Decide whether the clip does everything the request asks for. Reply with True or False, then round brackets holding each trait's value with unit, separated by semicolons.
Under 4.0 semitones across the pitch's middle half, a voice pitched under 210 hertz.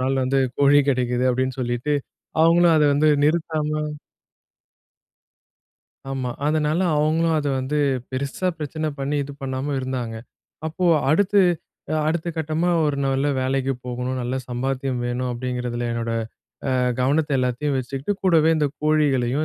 True (3.2 semitones; 135 Hz)